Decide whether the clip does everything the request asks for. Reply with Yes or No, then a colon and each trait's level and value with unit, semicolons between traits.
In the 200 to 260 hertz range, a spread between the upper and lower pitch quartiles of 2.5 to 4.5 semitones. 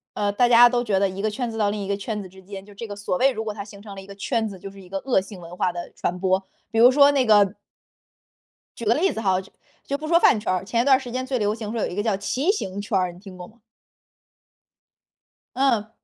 Yes: high, 210 Hz; average, 3.6 semitones